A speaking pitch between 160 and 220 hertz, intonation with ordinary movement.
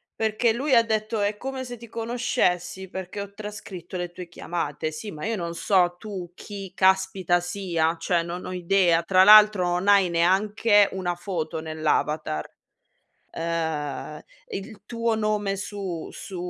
Yes: high, 190 Hz; average, 3.5 semitones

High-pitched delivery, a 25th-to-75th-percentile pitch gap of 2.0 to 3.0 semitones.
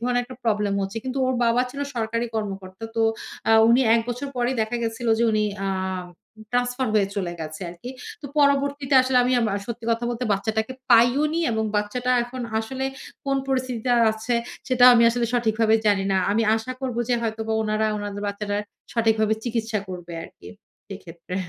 Yes: high, 230 Hz; average, 2.7 semitones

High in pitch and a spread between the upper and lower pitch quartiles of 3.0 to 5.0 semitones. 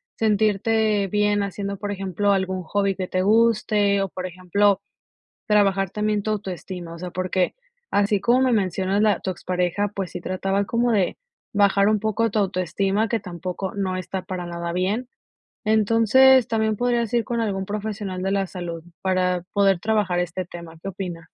No: high, 195 Hz; narrow, 2.5 semitones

